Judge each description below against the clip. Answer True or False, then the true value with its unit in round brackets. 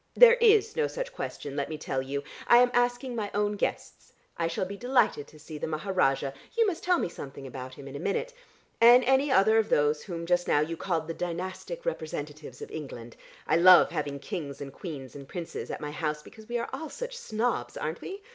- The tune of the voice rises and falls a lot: True (8.7 semitones)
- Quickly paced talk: True (220 wpm)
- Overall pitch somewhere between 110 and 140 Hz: False (175 Hz)